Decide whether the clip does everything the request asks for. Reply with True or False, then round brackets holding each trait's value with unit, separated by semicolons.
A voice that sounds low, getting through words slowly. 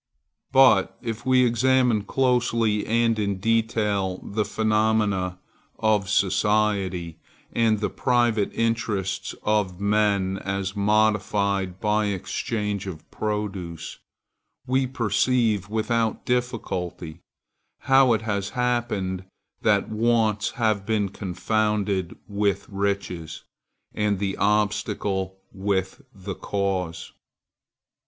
True (105 Hz; 95 wpm)